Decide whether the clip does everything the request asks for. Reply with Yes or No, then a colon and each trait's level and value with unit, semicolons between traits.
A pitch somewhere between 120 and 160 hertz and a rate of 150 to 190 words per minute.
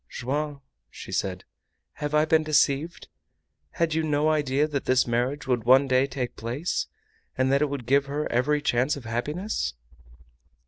Yes: medium, 140 Hz; average, 165 wpm